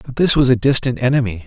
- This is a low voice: Yes, low, 125 Hz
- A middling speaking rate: No, fast, 245 wpm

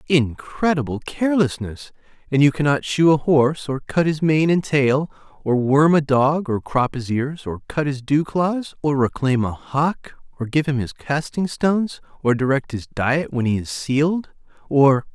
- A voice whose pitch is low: No, medium, 145 Hz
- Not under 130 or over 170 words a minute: No, average, 180 wpm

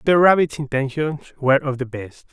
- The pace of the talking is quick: No, average, 180 wpm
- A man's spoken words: Yes, male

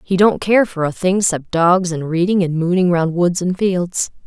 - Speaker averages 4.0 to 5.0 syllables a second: Yes, 4.5 syllables/s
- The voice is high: No, medium, 180 Hz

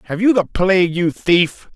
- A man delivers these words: Yes, male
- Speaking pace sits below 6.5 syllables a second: Yes, 4.6 syllables/s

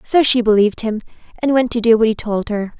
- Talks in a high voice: Yes, high, 225 Hz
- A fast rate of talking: Yes, fast, 260 wpm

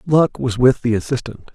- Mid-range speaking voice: No, low, 125 Hz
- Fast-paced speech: No, average, 195 wpm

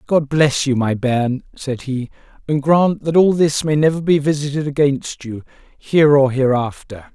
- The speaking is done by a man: Yes, male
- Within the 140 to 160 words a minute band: No, average, 175 wpm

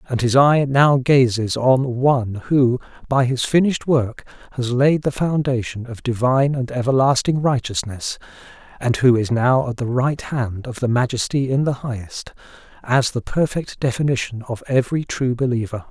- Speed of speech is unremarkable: Yes, average, 160 wpm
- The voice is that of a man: Yes, male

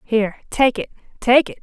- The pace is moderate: Yes, average, 150 wpm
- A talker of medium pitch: No, high, 240 Hz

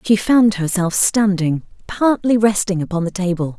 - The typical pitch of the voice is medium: No, high, 195 Hz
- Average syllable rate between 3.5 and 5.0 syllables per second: Yes, 4.7 syllables/s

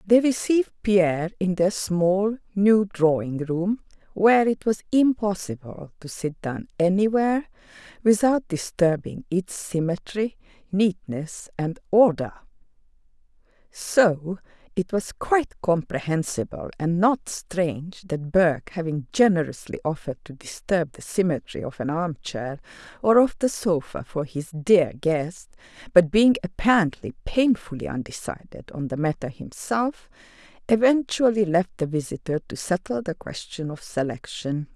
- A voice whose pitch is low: No, medium, 185 Hz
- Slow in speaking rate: Yes, slow, 125 wpm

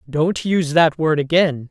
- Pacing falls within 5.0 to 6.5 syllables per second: No, 4.5 syllables/s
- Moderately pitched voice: Yes, medium, 160 Hz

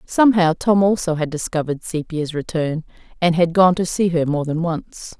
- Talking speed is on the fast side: No, average, 185 wpm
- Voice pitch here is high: No, medium, 170 Hz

